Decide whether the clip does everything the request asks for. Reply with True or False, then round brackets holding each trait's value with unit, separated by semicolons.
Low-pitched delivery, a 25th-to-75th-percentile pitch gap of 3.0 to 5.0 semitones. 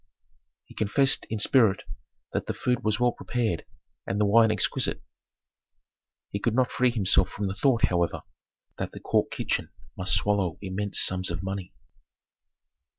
True (105 Hz; 3.5 semitones)